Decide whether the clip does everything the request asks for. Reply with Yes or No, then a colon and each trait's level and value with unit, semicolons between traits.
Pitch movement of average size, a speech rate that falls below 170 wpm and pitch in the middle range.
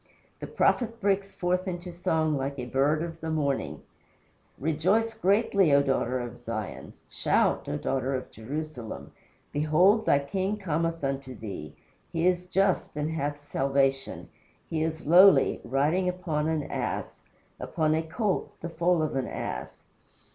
Yes: average, 4.8 semitones; average, 145 wpm; medium, 155 Hz